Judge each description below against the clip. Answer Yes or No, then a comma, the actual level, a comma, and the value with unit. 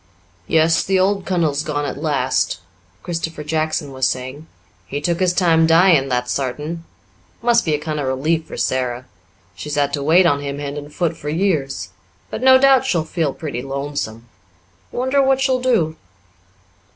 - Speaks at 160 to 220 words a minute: Yes, average, 170 wpm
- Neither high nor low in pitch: Yes, medium, 155 Hz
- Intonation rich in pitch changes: No, average, 3.8 semitones